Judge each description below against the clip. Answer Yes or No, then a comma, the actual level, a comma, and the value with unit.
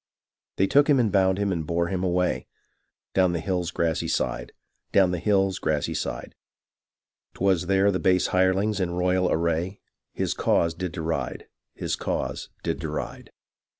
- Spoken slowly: No, average, 155 wpm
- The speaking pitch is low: Yes, very low, 90 Hz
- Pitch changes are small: Yes, narrow, 2.1 semitones